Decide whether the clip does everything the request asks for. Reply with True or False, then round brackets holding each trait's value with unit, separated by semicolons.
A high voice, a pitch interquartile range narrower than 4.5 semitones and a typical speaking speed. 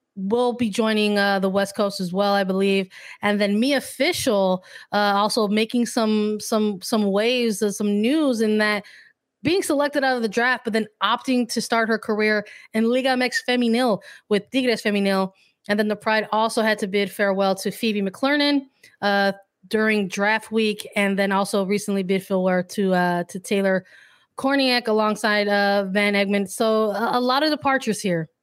True (210 Hz; 2.8 semitones; 180 wpm)